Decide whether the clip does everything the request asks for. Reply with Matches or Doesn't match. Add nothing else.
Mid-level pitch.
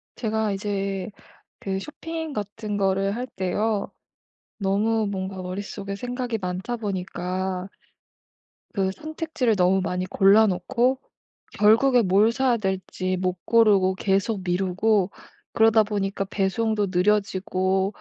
Doesn't match